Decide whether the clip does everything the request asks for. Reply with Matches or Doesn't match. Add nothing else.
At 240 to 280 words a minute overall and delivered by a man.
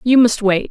Doesn't match